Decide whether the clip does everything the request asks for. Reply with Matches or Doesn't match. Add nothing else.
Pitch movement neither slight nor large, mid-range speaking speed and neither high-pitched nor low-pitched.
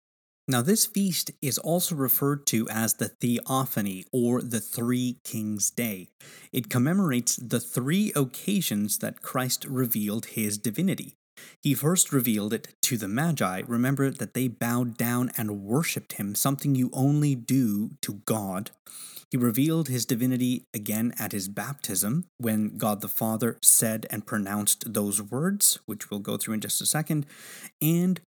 Doesn't match